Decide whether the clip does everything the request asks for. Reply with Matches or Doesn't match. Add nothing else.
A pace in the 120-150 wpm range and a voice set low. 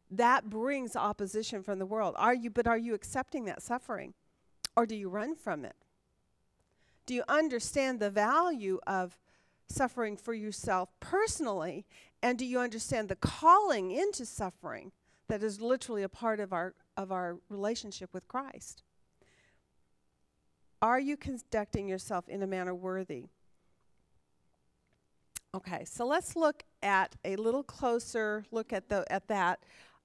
Doesn't match